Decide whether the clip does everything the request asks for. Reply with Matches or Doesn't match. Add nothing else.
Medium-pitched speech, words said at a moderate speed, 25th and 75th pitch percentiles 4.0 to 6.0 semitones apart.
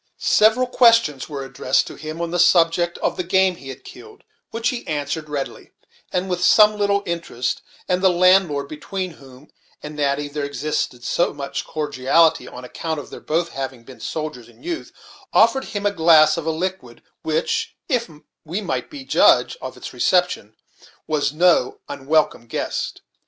Matches